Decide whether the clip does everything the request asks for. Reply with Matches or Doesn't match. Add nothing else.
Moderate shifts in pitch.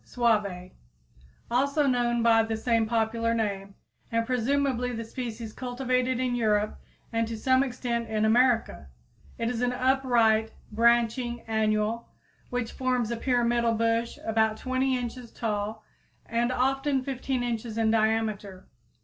Doesn't match